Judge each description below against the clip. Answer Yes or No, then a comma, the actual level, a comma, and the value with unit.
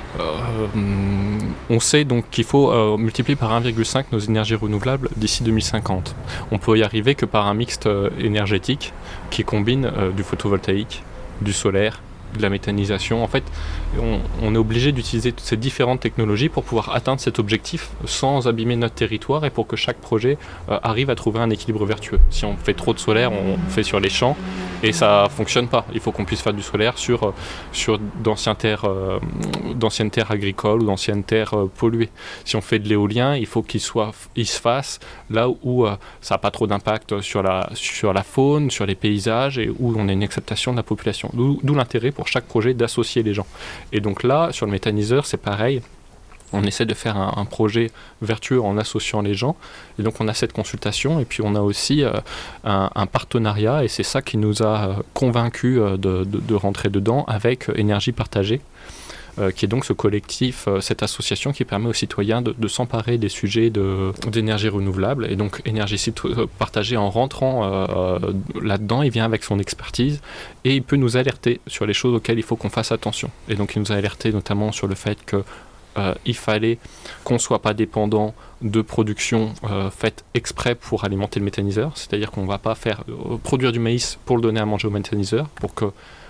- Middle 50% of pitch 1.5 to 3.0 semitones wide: Yes, average, 2.7 semitones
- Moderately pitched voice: No, low, 110 Hz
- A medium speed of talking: Yes, average, 200 wpm